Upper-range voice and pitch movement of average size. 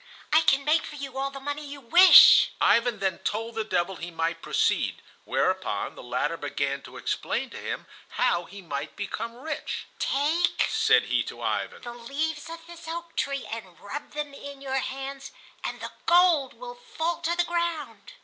No: very high, 275 Hz; wide, 7.2 semitones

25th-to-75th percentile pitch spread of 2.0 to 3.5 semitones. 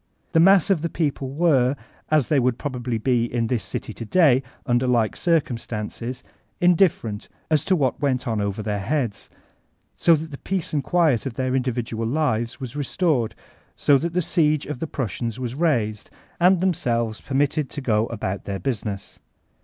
No: average, 5.1 semitones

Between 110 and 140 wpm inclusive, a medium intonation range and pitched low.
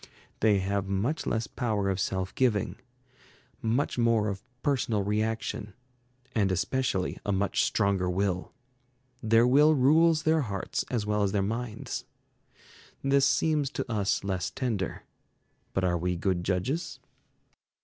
Yes: slow, 135 wpm; average, 4.6 semitones; low, 105 Hz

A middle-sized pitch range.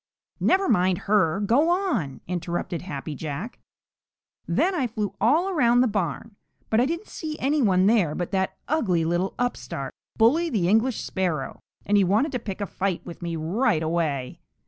No: wide, 6.4 semitones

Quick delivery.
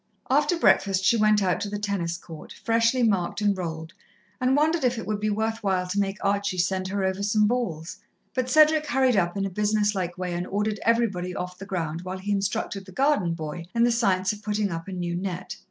Yes: fast, 225 wpm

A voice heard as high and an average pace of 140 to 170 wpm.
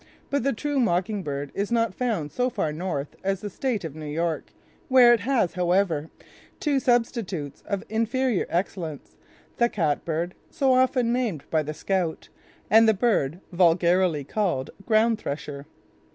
Yes: high, 195 Hz; average, 150 wpm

